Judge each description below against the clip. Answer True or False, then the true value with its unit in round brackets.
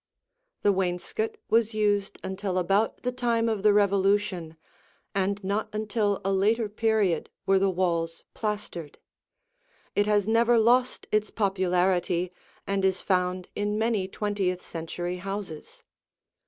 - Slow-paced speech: True (125 wpm)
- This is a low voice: False (200 Hz)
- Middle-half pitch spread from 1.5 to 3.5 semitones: True (2.6 semitones)